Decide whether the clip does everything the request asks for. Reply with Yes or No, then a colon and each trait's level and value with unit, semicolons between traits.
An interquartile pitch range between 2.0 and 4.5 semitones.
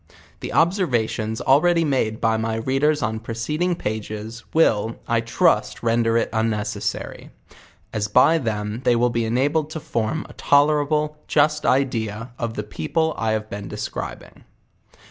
No: average, 5.3 semitones